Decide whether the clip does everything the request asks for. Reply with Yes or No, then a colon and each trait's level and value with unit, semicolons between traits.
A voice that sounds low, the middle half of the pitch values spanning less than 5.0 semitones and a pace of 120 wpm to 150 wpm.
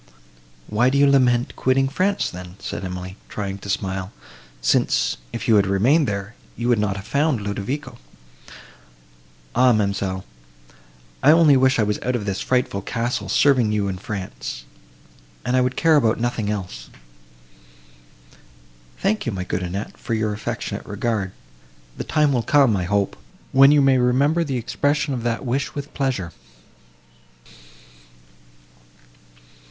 No: low, 115 Hz; average, 5.3 semitones; average, 145 wpm